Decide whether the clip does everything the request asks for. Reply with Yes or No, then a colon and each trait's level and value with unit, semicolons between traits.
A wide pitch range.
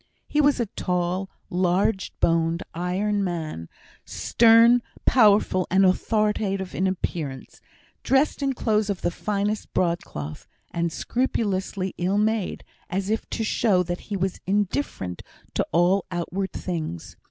No: average, 3.3 semitones